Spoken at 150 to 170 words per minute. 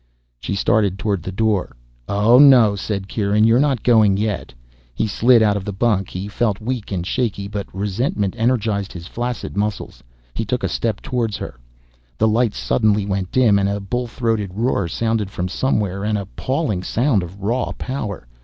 No: average, 180 wpm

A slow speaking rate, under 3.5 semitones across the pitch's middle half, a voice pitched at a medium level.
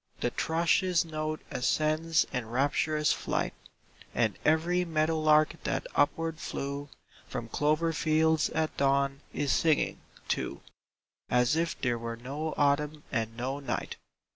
Yes: slow, 130 wpm; narrow, 2.5 semitones; medium, 150 Hz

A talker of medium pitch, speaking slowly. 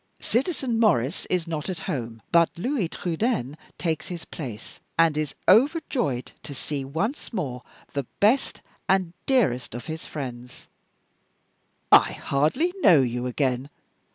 Yes: medium, 160 Hz; slow, 130 wpm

